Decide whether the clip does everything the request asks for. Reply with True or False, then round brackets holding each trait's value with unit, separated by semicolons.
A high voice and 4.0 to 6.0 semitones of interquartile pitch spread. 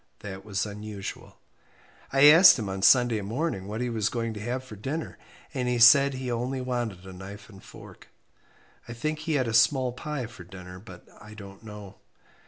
False (115 Hz; 4.3 semitones)